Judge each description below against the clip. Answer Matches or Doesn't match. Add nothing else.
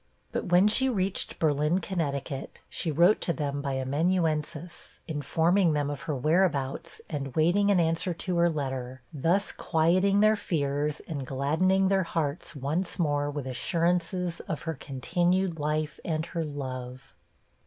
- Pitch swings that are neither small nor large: Matches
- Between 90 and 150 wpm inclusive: Matches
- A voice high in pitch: Doesn't match